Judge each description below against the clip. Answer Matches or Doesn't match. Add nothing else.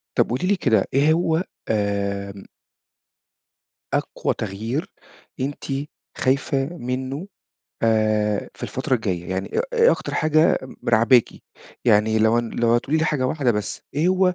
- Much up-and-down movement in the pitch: Matches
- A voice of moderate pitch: Doesn't match